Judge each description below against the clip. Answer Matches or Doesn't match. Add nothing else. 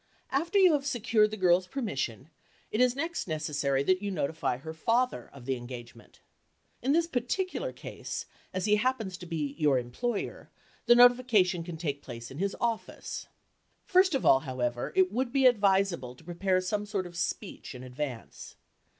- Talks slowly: Doesn't match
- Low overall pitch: Doesn't match